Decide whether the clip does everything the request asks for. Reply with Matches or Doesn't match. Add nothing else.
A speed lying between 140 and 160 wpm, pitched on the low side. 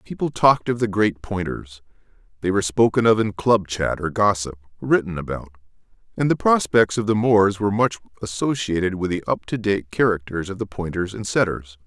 Doesn't match